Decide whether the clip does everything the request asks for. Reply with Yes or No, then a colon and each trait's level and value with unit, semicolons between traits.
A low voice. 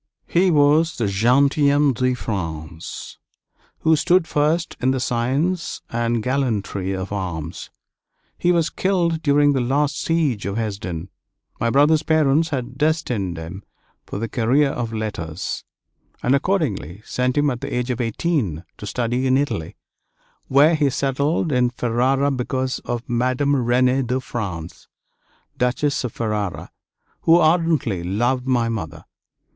Yes: low, 125 Hz